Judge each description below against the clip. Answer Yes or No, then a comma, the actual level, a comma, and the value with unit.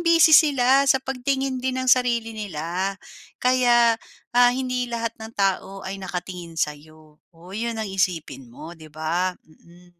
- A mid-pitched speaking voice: No, high, 220 Hz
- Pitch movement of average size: No, wide, 6.5 semitones